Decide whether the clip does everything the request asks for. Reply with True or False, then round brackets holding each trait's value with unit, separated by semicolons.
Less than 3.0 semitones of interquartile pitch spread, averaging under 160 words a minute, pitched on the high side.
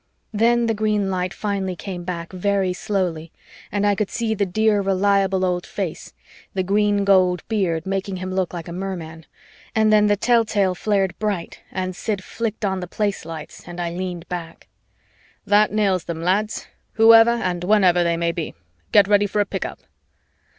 False (2.6 semitones; 180 wpm; 195 Hz)